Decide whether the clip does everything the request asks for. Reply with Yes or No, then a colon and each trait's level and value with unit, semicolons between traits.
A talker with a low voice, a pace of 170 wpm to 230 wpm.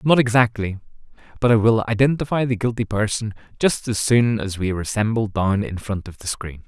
Yes: low, 110 Hz; average, 200 wpm